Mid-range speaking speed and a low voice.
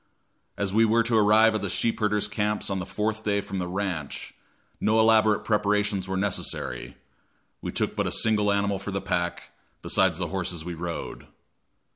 Yes: average, 180 wpm; low, 105 Hz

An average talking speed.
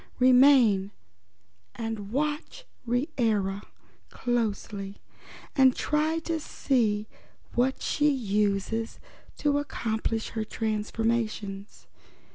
No: slow, 80 wpm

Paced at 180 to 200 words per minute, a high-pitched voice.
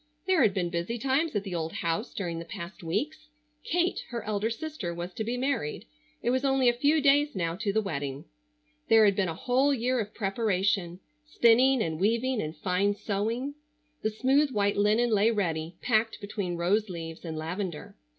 Yes: average, 190 wpm; high, 210 Hz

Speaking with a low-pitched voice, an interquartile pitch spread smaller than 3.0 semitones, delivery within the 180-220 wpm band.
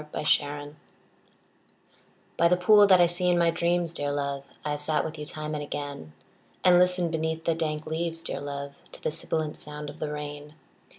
No: medium, 155 Hz; narrow, 2.5 semitones; average, 195 wpm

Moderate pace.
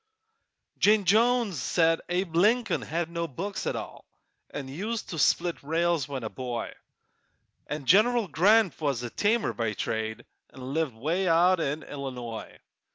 Yes: average, 150 wpm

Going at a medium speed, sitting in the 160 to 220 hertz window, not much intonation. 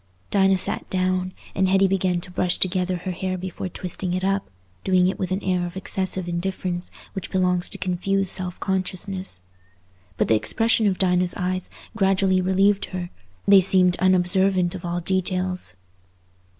Yes: average, 160 wpm; medium, 185 Hz; narrow, 1.0 semitones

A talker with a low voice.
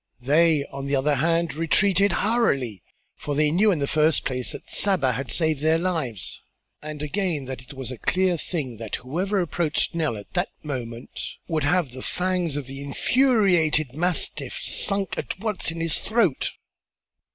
No: medium, 155 Hz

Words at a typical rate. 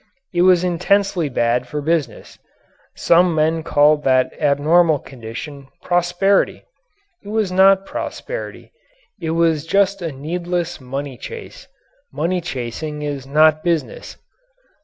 No: slow, 115 wpm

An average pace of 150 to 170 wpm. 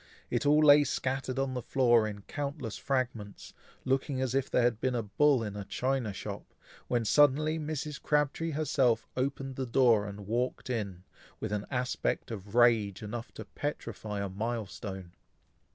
Yes: average, 165 wpm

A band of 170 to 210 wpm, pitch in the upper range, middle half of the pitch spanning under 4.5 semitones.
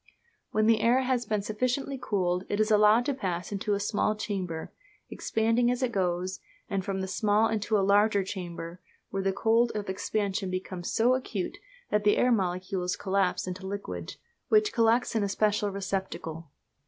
Yes: average, 175 wpm; high, 205 Hz; average, 2.9 semitones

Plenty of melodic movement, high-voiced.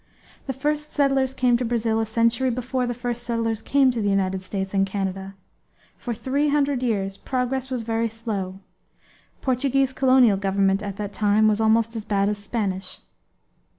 No: average, 4.2 semitones; high, 230 Hz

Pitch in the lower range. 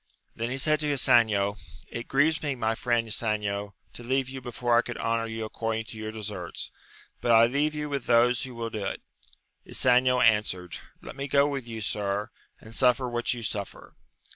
Yes: low, 115 Hz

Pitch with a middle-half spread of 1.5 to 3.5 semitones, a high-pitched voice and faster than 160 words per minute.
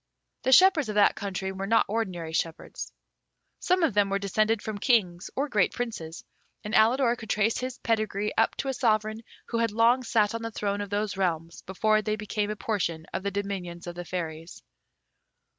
Yes: average, 3.1 semitones; high, 210 Hz; average, 190 wpm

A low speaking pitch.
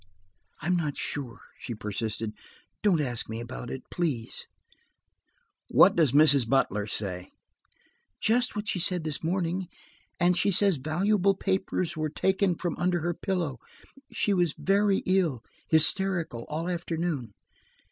No: medium, 165 Hz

